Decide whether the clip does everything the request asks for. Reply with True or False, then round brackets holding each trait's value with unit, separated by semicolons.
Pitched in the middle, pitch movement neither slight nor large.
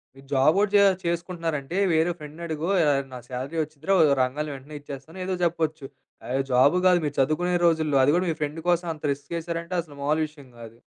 True (155 Hz; 3.3 semitones)